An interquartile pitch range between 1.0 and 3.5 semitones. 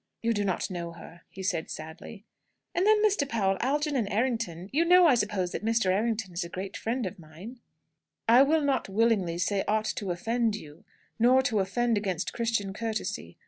No: average, 4.4 semitones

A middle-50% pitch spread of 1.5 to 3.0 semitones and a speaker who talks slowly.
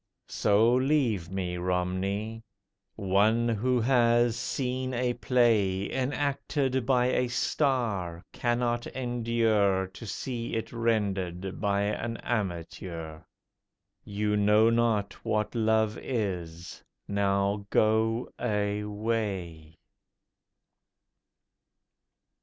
No: average, 3.4 semitones; slow, 85 wpm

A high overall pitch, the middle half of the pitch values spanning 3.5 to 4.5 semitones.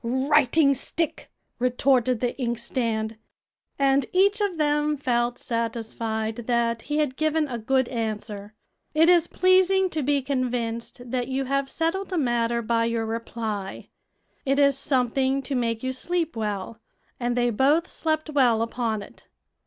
Yes: very high, 255 Hz; average, 4.1 semitones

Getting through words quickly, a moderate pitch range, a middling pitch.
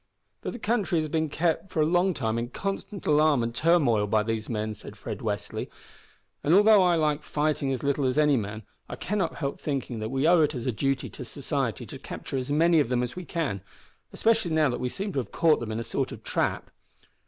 No: fast, 235 wpm; wide, 5.7 semitones; medium, 145 Hz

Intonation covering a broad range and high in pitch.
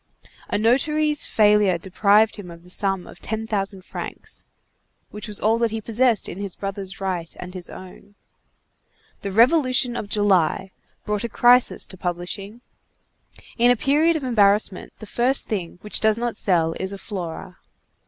No: average, 3.6 semitones; high, 205 Hz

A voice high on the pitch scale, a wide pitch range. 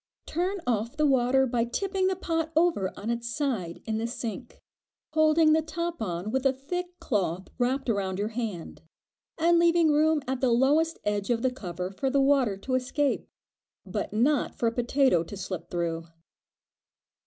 Yes: very high, 255 Hz; wide, 6.5 semitones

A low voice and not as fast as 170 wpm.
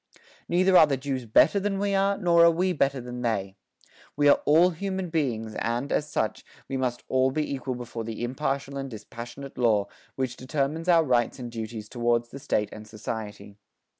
No: low, 130 Hz; average, 190 wpm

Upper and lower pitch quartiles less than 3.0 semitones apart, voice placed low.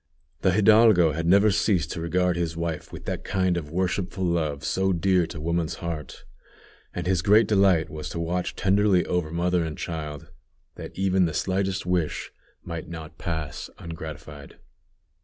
Yes: narrow, 2.6 semitones; very low, 85 Hz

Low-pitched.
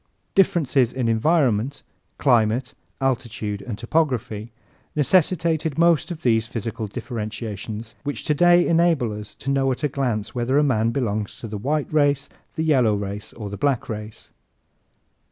Yes: low, 125 Hz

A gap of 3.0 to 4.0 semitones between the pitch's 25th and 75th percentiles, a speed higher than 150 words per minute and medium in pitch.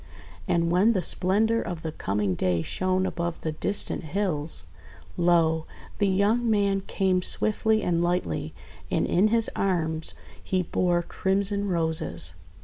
No: average, 3.7 semitones; average, 140 wpm; medium, 180 Hz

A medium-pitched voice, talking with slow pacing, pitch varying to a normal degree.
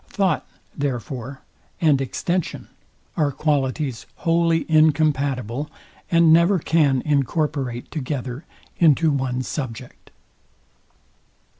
Yes: medium, 145 Hz; slow, 85 wpm; average, 3.7 semitones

